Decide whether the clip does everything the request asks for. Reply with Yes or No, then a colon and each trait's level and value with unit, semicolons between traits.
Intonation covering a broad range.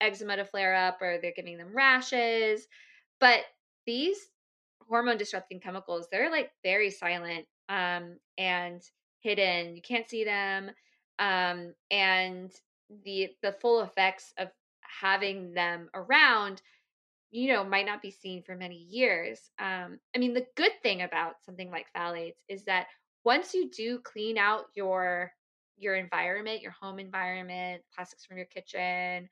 No: average, 3.0 semitones